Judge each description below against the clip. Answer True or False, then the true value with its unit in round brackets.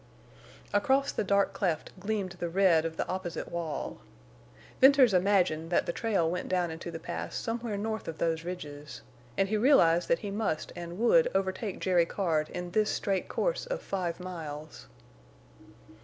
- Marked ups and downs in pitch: False (3.8 semitones)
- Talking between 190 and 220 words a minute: False (165 wpm)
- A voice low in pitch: False (185 Hz)